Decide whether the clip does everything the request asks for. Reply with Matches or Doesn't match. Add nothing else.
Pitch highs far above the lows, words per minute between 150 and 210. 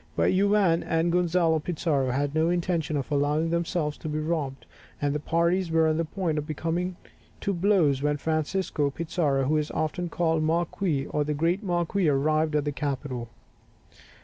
Doesn't match